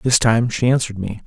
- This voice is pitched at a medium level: No, low, 115 Hz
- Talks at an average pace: No, fast, 235 wpm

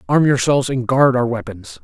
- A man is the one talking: Yes, male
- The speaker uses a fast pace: No, average, 195 wpm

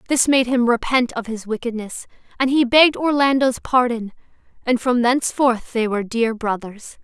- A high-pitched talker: Yes, high, 240 Hz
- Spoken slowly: No, average, 160 wpm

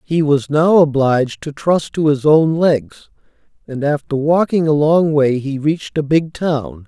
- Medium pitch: Yes, medium, 150 Hz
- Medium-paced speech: Yes, average, 185 wpm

